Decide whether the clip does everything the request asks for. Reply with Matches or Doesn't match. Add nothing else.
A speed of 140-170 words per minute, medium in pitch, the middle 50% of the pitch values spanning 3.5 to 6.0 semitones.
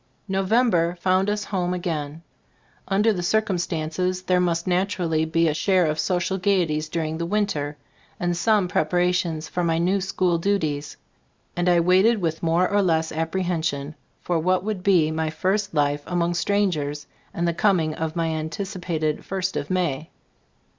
Doesn't match